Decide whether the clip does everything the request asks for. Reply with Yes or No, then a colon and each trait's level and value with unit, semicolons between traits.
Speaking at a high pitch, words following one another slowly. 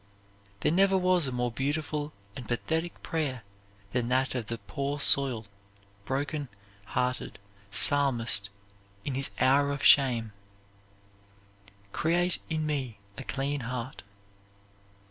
No: low, 135 Hz; slow, 115 wpm